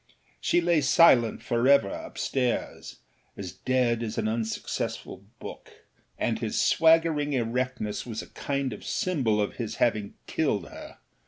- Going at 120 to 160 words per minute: Yes, slow, 135 wpm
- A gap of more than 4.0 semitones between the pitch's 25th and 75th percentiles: Yes, average, 4.5 semitones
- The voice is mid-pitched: No, low, 125 Hz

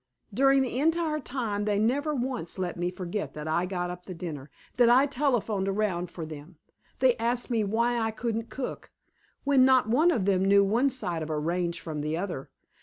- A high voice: Yes, high, 210 Hz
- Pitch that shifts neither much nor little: No, wide, 6.2 semitones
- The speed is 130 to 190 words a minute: No, average, 200 wpm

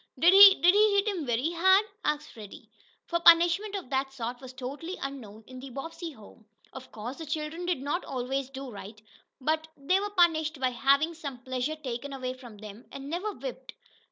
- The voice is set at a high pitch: Yes, very high, 280 Hz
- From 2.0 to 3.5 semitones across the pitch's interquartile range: No, average, 5.1 semitones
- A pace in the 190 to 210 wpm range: Yes, average, 195 wpm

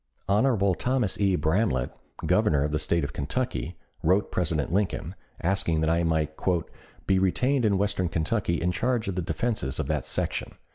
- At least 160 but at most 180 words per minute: Yes, average, 170 wpm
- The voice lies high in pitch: No, very low, 90 Hz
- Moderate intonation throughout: Yes, average, 4.6 semitones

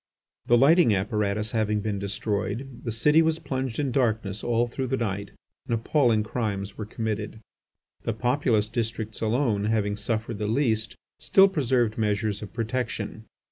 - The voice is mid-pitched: No, low, 110 Hz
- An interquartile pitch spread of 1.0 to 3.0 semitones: Yes, average, 2.7 semitones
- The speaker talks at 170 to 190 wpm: No, average, 150 wpm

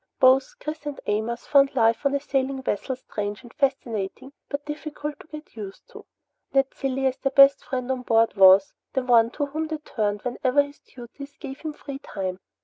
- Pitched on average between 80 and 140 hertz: No, very high, 265 Hz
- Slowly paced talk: No, average, 195 wpm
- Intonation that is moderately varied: Yes, average, 3.7 semitones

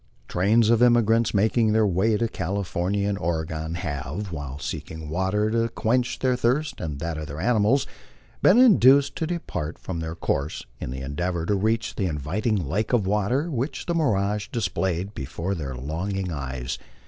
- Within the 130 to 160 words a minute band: No, average, 170 wpm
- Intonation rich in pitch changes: Yes, wide, 6.1 semitones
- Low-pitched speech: Yes, low, 100 Hz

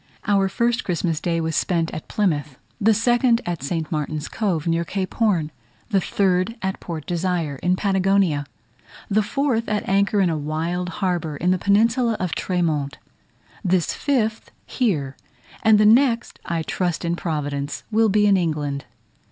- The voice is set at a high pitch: No, medium, 180 Hz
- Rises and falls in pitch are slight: No, average, 4.7 semitones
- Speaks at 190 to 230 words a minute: No, average, 160 wpm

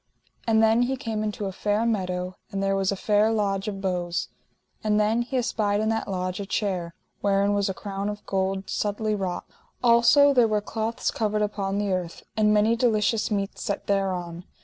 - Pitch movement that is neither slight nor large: No, narrow, 2.1 semitones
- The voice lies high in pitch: Yes, high, 205 Hz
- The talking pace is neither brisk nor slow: Yes, average, 195 wpm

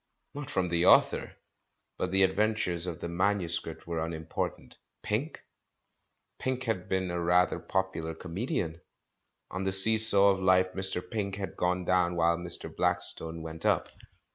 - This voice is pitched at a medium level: No, very low, 90 Hz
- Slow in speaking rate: No, average, 150 wpm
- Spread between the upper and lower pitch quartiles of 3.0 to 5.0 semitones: No, narrow, 2.4 semitones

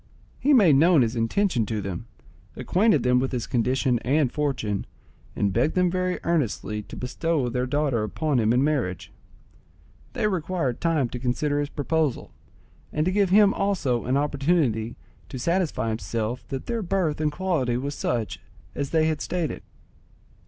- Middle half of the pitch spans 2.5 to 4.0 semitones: No, wide, 5.6 semitones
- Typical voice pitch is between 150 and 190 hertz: No, medium, 140 Hz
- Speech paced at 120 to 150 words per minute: No, average, 160 wpm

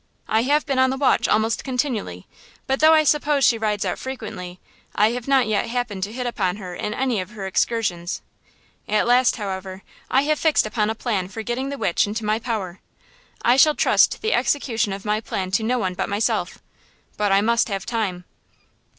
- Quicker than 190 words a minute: Yes, average, 200 wpm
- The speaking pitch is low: No, high, 220 Hz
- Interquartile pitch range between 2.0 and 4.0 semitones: No, average, 4.5 semitones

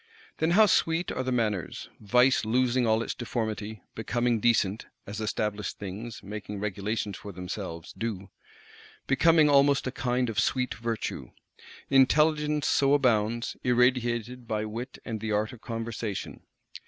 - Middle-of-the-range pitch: No, low, 115 Hz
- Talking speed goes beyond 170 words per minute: No, average, 140 wpm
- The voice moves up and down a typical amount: Yes, average, 3.3 semitones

